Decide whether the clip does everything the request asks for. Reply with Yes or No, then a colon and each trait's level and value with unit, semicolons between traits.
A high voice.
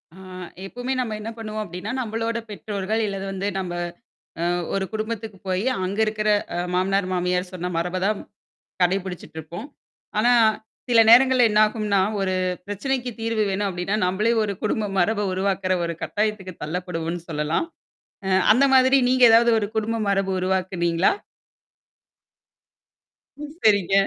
Yes: high, 200 Hz